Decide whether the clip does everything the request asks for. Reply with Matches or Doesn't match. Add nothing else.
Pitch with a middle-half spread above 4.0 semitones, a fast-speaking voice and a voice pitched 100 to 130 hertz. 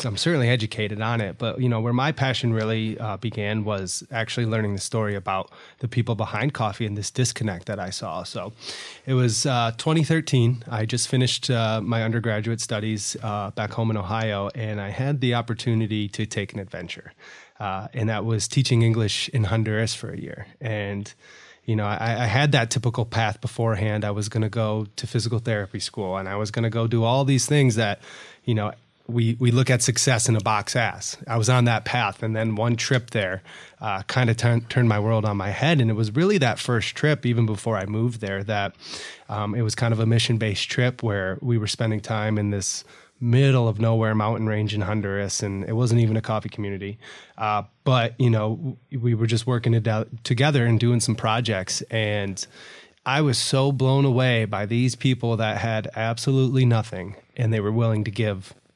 Doesn't match